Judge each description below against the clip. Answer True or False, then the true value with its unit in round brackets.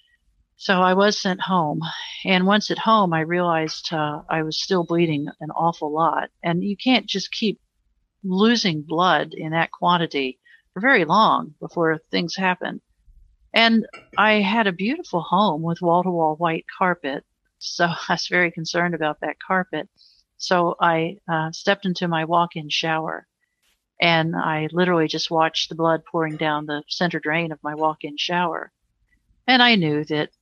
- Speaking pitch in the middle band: True (170 Hz)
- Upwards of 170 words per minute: False (160 wpm)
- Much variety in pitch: False (2.8 semitones)